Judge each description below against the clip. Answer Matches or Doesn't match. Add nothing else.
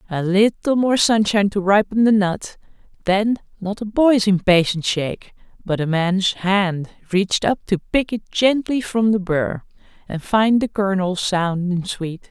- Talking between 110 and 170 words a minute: Matches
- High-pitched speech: Matches